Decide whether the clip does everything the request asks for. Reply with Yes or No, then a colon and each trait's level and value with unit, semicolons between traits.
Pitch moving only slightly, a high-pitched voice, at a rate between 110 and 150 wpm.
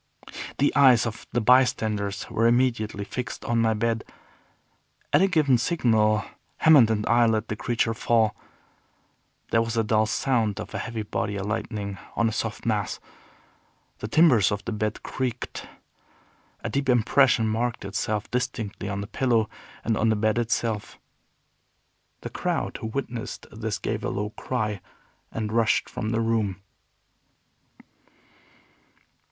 No: narrow, 2.0 semitones; low, 110 Hz; average, 145 wpm